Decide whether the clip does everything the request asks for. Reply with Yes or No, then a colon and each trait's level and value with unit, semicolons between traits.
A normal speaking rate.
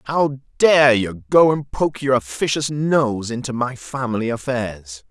Yes: average, 155 wpm